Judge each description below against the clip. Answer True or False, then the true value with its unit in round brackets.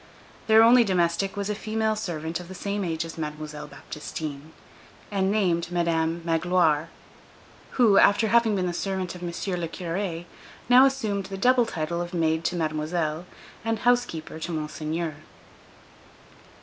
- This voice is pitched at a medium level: True (175 Hz)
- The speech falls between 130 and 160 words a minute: True (150 wpm)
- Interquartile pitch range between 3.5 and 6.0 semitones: True (4.0 semitones)